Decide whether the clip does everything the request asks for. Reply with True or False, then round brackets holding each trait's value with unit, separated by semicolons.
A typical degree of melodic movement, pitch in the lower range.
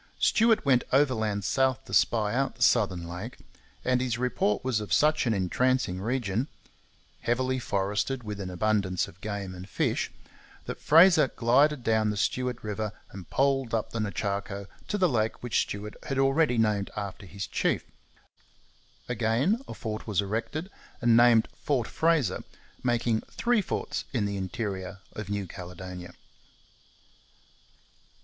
True (4.4 semitones; 110 Hz)